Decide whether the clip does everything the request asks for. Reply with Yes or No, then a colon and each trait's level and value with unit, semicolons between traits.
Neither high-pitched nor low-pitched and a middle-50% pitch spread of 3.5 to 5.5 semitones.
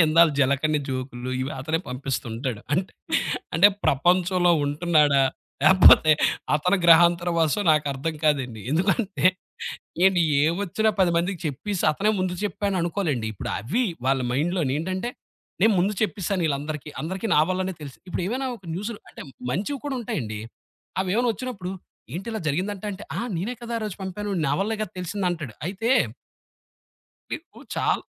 Yes: medium, 175 Hz; average, 5.1 semitones